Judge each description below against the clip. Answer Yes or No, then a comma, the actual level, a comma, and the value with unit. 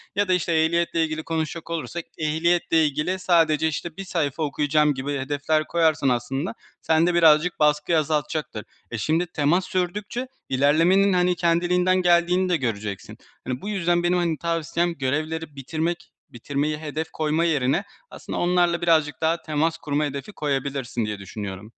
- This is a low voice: No, medium, 160 Hz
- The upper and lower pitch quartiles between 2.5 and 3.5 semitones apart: Yes, average, 3.0 semitones